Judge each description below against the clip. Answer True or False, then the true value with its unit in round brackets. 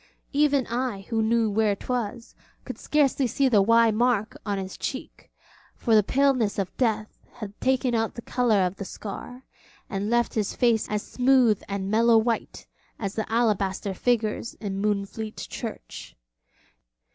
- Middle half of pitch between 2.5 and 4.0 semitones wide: True (3.0 semitones)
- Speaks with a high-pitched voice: True (225 Hz)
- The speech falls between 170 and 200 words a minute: False (155 wpm)